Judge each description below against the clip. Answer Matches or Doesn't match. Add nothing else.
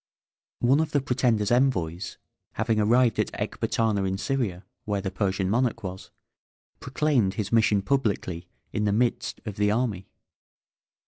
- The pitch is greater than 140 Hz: Doesn't match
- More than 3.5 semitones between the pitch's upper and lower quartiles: Matches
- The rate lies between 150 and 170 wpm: Doesn't match